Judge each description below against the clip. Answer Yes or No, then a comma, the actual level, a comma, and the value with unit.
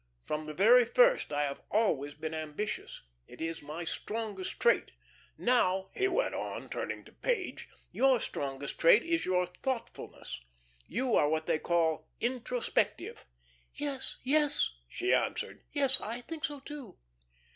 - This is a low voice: No, high, 225 Hz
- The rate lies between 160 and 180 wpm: No, average, 145 wpm